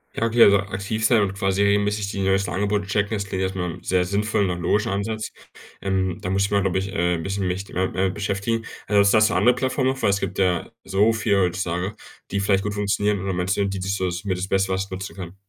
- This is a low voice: Yes, low, 100 Hz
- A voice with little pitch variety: Yes, narrow, 1.5 semitones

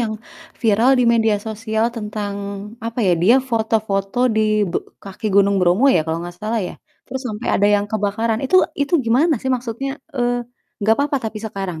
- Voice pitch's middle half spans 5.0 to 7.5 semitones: No, average, 2.7 semitones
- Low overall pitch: No, high, 220 Hz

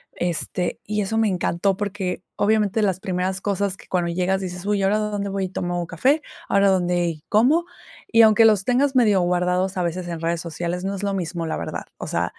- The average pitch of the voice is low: No, high, 190 Hz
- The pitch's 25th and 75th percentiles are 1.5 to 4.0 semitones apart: Yes, average, 2.7 semitones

